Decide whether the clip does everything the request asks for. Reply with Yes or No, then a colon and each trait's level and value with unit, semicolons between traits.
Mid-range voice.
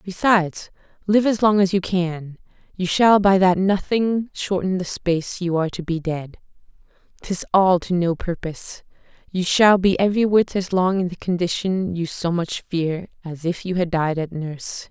Yes: medium, 180 Hz